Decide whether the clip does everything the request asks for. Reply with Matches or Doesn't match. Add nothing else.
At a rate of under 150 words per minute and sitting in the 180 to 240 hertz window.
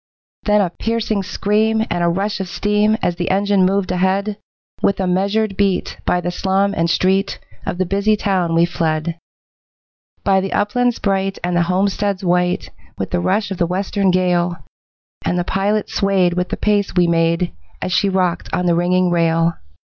Doesn't match